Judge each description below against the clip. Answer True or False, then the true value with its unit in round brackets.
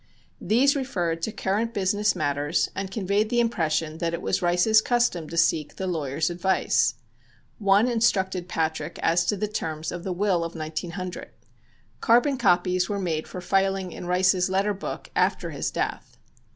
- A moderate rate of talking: True (165 wpm)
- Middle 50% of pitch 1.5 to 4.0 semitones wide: True (3.6 semitones)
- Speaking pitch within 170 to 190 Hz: True (185 Hz)